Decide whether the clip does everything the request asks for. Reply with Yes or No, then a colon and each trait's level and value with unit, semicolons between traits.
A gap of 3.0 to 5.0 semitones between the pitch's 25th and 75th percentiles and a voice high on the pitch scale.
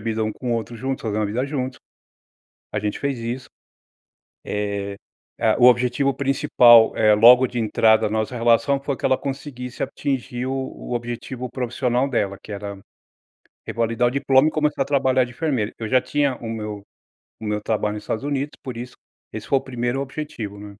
No: average, 3.4 semitones; low, 120 Hz